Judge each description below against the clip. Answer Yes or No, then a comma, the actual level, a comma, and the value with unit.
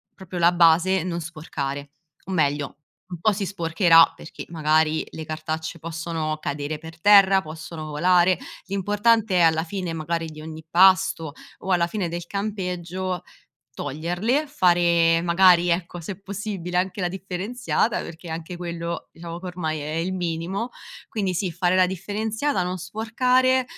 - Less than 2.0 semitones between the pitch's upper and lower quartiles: No, average, 2.7 semitones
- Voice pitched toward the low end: No, medium, 175 Hz